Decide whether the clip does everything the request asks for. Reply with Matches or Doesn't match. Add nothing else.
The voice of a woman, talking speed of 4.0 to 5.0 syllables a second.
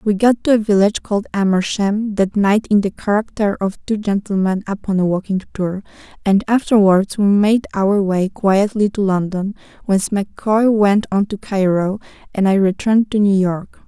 Matches